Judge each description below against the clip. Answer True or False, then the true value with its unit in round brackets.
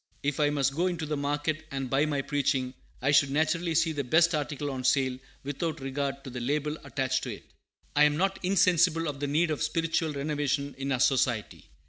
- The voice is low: False (145 Hz)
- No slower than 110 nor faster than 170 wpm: False (205 wpm)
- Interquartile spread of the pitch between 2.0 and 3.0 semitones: True (2.5 semitones)